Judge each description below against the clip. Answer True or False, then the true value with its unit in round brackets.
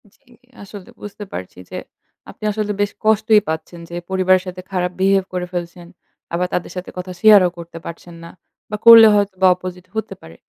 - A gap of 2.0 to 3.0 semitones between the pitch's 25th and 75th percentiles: True (2.6 semitones)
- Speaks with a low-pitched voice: False (185 Hz)